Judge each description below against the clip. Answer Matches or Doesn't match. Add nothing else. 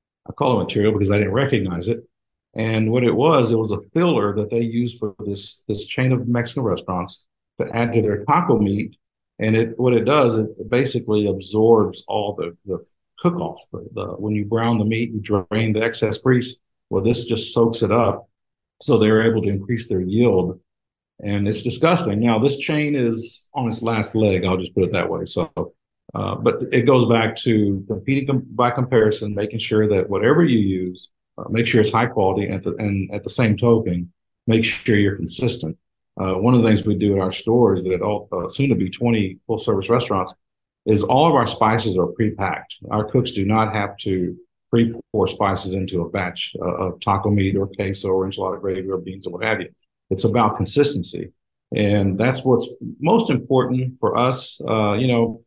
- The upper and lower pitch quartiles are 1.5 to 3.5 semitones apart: Matches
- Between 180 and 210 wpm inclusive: Matches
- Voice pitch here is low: Matches